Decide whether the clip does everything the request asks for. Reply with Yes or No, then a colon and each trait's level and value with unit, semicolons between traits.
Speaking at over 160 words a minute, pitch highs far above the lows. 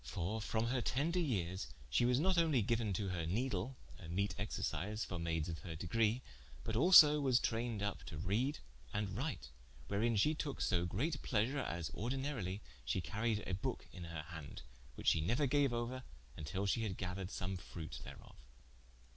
Yes: average, 180 wpm; wide, 6.0 semitones